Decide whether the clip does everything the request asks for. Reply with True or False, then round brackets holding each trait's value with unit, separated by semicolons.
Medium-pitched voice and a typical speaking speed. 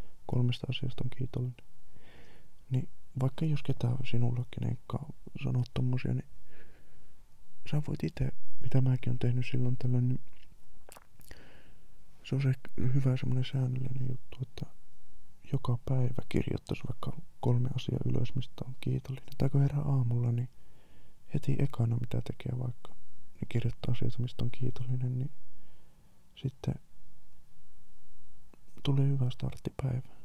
False (125 Hz; 125 wpm)